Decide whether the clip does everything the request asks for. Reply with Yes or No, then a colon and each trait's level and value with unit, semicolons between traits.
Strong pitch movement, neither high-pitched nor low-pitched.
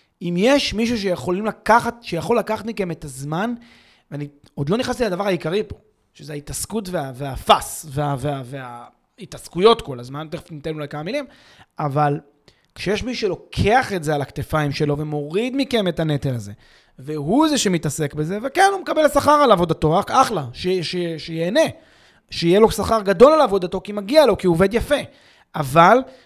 Yes: wide, 7.4 semitones; medium, 180 Hz